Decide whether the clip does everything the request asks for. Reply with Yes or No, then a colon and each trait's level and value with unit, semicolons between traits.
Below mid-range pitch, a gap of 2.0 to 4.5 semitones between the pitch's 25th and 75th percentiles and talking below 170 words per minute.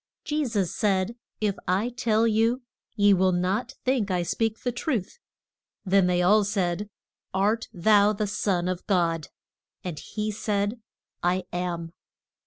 No: high, 205 Hz; average, 3.5 semitones; average, 145 wpm